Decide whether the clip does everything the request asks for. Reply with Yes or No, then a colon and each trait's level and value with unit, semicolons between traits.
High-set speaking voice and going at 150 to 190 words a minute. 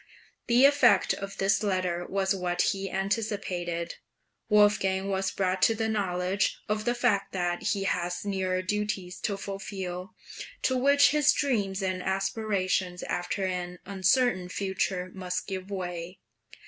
No: high, 195 Hz; slow, 135 wpm